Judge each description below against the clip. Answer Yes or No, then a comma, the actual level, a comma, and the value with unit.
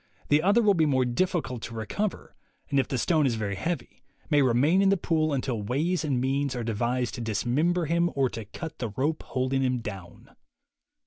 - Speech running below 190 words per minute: No, average, 200 wpm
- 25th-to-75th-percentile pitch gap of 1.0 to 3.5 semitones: No, average, 5.2 semitones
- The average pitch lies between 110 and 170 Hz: Yes, low, 135 Hz